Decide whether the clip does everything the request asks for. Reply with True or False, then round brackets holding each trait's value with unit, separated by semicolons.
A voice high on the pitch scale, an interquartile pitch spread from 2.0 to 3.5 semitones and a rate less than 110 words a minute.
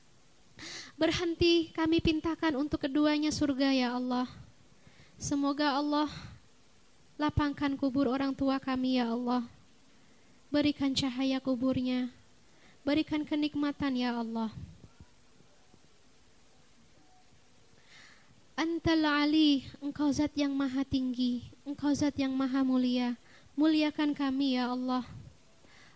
True (280 Hz; 2.4 semitones; 90 wpm)